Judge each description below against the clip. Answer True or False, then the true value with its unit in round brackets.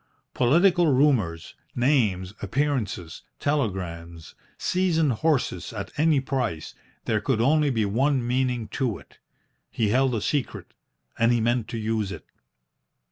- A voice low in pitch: True (120 Hz)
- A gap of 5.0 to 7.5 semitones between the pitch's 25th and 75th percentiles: True (5.4 semitones)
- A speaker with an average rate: False (130 wpm)